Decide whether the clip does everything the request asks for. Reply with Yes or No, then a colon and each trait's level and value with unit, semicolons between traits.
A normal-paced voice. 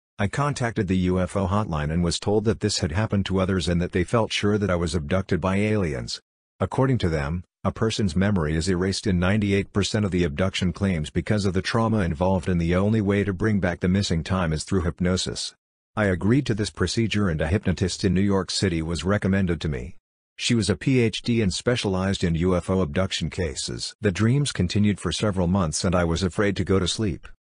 No: fast, 210 wpm